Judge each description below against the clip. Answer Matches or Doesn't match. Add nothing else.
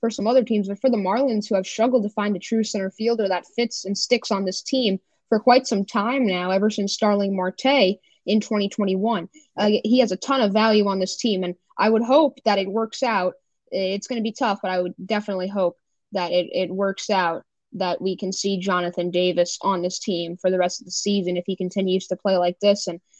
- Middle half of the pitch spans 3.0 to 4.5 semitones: Matches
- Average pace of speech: Doesn't match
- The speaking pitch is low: Doesn't match